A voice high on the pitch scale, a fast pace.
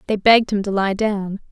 Yes: high, 205 Hz; fast, 235 wpm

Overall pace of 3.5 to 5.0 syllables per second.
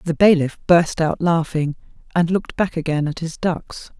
Yes: 4.8 syllables/s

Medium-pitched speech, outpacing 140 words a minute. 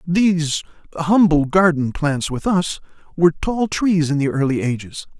Yes: medium, 165 Hz; average, 150 wpm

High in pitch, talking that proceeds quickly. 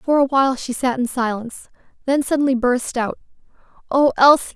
No: very high, 260 Hz; average, 170 wpm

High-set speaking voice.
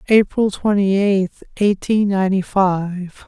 Yes: high, 195 Hz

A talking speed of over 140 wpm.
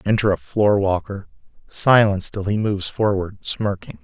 No: slow, 135 wpm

